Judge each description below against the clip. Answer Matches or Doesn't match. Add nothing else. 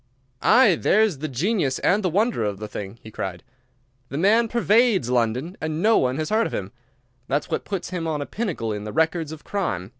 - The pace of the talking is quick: Matches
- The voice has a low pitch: Doesn't match